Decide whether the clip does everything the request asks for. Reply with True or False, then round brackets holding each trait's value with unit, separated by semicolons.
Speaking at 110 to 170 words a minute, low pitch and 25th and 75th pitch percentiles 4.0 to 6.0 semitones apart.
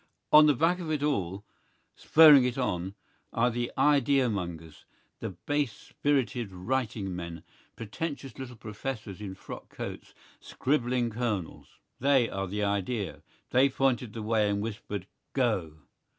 True (135 wpm; 115 Hz; 5.2 semitones)